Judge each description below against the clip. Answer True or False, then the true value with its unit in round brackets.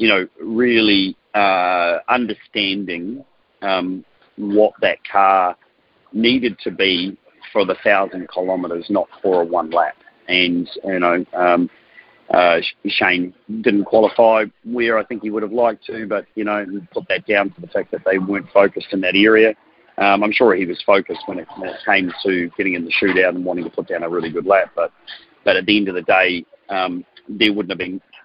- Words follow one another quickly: False (190 wpm)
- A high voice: False (95 Hz)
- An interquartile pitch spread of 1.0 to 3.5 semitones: True (2.9 semitones)